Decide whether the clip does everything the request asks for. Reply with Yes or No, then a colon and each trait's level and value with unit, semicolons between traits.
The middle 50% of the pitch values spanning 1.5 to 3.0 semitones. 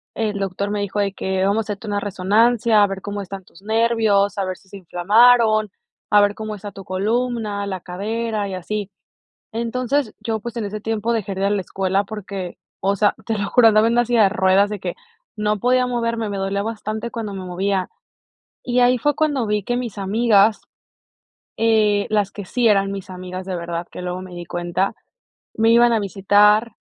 Yes: narrow, 2.6 semitones